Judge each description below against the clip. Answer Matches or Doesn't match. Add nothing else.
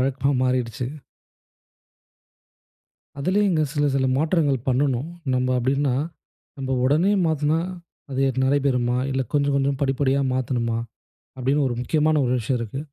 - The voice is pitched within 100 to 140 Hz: Matches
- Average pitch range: Doesn't match